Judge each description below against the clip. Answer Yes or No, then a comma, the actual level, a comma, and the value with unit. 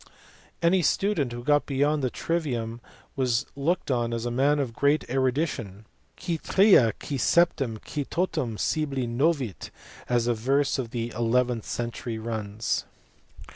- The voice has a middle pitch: No, low, 130 Hz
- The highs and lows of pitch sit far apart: No, average, 4.0 semitones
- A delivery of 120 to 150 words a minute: Yes, average, 140 wpm